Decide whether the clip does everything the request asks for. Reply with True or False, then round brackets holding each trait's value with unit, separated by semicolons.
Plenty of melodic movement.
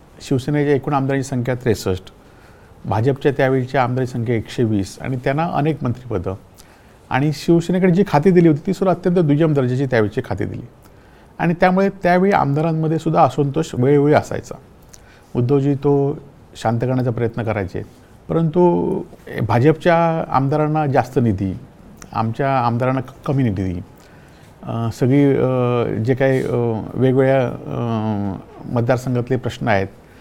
False (4.4 semitones)